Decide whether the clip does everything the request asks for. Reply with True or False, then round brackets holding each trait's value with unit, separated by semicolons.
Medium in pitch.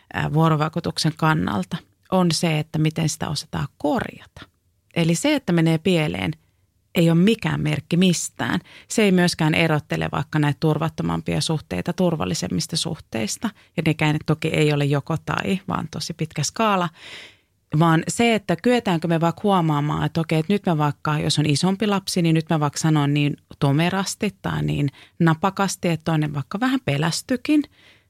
True (160 Hz)